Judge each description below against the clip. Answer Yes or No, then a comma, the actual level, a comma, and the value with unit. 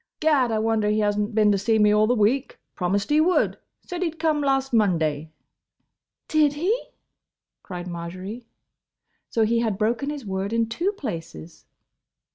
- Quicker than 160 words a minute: Yes, average, 170 wpm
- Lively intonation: Yes, wide, 5.7 semitones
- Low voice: No, high, 220 Hz